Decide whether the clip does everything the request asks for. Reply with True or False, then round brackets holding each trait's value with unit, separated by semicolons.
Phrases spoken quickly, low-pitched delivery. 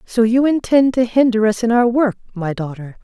False (215 wpm; 230 Hz)